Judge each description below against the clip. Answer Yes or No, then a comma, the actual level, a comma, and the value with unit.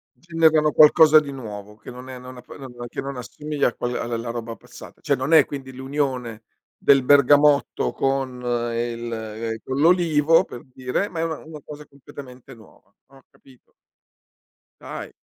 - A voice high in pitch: No, low, 135 Hz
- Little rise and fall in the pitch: No, average, 3.5 semitones